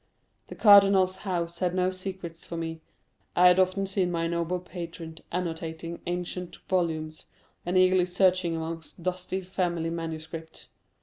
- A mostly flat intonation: Yes, narrow, 1.9 semitones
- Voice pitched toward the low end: No, medium, 175 Hz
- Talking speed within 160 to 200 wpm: No, slow, 135 wpm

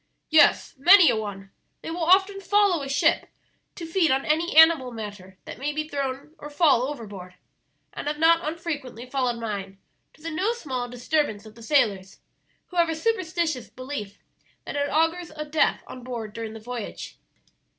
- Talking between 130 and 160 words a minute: No, average, 175 wpm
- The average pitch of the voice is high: Yes, very high, 285 Hz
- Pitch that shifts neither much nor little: No, wide, 6.0 semitones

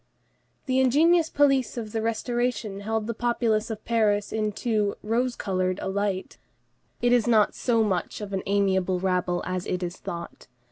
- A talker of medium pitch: No, high, 215 Hz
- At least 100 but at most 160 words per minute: No, average, 170 wpm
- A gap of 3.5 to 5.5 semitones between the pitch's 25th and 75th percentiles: Yes, average, 3.8 semitones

